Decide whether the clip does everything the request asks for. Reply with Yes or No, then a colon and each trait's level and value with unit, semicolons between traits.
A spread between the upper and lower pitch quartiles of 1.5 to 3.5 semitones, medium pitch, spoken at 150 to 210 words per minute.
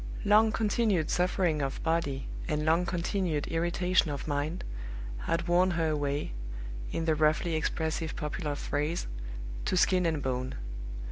No: average, 3.1 semitones; medium, 165 Hz; slow, 135 wpm